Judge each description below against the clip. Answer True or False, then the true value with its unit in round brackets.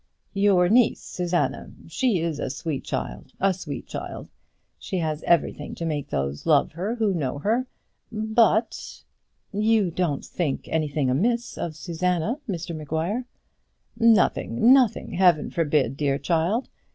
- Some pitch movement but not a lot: False (5.9 semitones)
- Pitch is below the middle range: False (175 Hz)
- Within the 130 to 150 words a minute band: True (140 wpm)